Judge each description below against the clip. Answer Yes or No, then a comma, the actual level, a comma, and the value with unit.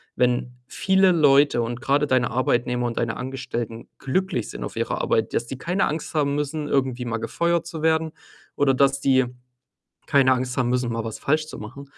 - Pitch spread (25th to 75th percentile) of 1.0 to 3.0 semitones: No, average, 3.6 semitones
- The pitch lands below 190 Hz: Yes, low, 135 Hz